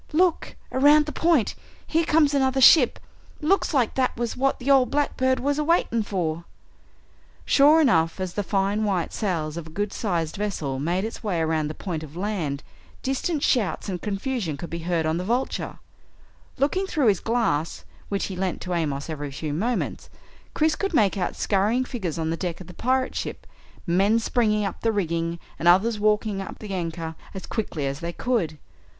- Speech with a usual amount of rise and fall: No, wide, 7.4 semitones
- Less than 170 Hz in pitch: No, high, 200 Hz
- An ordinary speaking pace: Yes, average, 190 wpm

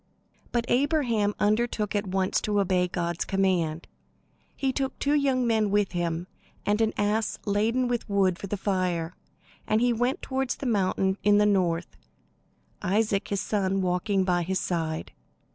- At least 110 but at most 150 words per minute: No, average, 160 wpm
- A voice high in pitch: Yes, high, 205 Hz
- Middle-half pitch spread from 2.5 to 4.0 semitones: Yes, average, 3.6 semitones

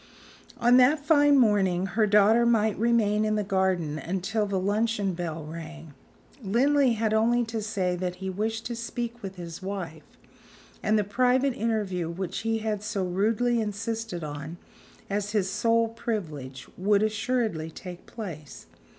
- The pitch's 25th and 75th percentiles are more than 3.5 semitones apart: Yes, average, 3.9 semitones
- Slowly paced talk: No, average, 150 wpm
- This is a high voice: Yes, high, 210 Hz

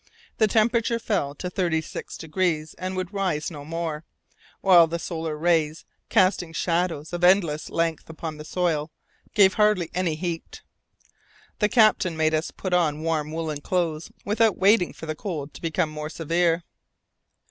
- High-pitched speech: No, medium, 165 Hz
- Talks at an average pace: Yes, average, 155 wpm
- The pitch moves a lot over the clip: No, average, 2.9 semitones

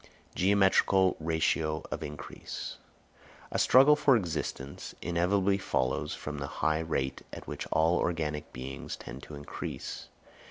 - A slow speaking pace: Yes, slow, 125 wpm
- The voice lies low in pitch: Yes, very low, 80 Hz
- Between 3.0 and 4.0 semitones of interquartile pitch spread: No, average, 4.4 semitones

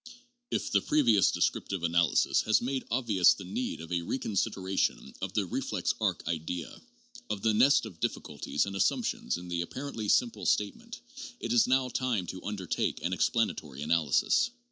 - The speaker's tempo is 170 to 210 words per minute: No, average, 160 wpm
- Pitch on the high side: No, low, 100 Hz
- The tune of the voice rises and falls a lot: Yes, wide, 5.8 semitones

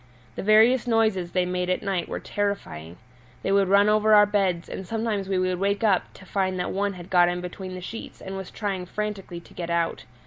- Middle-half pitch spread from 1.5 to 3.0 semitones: Yes, narrow, 2.4 semitones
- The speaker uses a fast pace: Yes, fast, 220 wpm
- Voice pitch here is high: Yes, high, 195 Hz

